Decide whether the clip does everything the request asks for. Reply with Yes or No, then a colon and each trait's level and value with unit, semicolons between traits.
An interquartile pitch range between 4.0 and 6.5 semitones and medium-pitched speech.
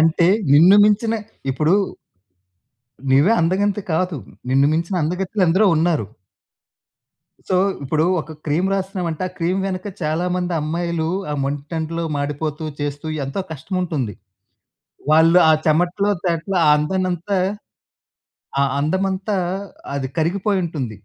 No: average, 3.5 semitones; medium, 170 Hz